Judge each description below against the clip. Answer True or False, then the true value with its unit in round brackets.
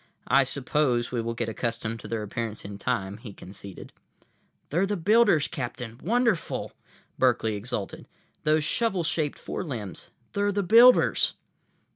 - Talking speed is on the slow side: True (130 wpm)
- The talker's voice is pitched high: False (125 Hz)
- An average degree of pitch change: False (7.4 semitones)